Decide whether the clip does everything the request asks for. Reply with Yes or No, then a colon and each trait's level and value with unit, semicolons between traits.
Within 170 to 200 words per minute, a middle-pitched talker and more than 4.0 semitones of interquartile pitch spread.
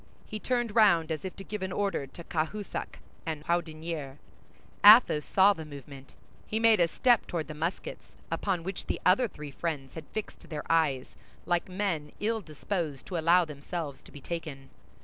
Yes: average, 175 wpm; medium, 170 Hz; average, 4.7 semitones